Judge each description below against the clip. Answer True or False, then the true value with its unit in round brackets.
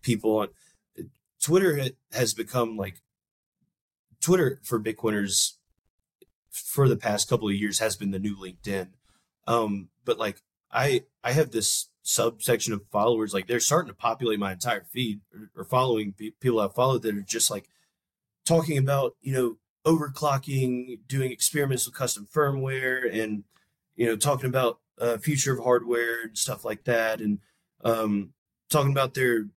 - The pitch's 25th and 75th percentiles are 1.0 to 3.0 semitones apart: False (3.9 semitones)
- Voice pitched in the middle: False (120 Hz)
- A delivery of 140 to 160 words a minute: True (155 wpm)